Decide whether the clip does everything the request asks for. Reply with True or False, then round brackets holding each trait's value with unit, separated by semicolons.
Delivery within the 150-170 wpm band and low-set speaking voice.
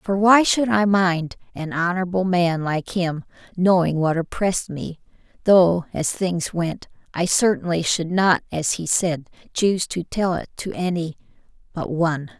False (160 wpm; 175 Hz)